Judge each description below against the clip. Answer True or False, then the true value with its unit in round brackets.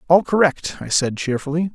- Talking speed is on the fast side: False (170 wpm)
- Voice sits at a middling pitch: True (160 Hz)